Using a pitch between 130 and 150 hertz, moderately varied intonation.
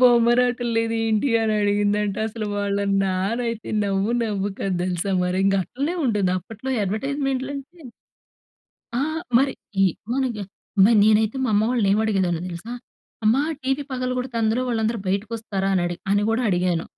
No: high, 220 Hz; average, 3.8 semitones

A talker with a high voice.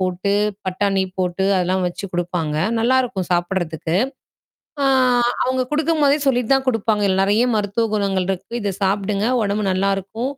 Yes: high, 200 Hz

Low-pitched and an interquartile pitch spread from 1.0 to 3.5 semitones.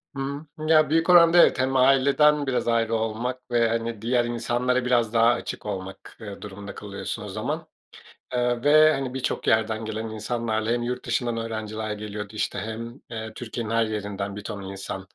Yes: low, 115 Hz; average, 2.7 semitones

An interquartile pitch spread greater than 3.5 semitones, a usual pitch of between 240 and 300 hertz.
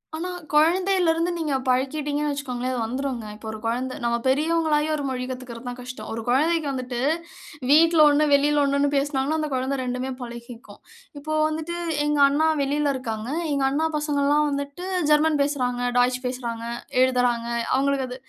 No: average, 3.1 semitones; very high, 280 Hz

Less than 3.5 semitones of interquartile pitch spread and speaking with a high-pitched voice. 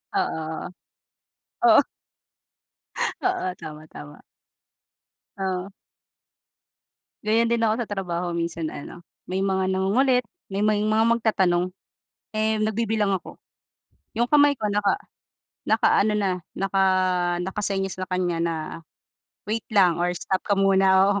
Yes: average, 3.1 semitones; high, 195 Hz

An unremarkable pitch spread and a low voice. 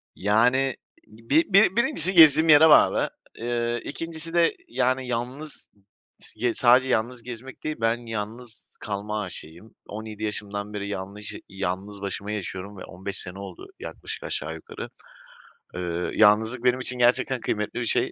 Yes: average, 4.2 semitones; low, 115 Hz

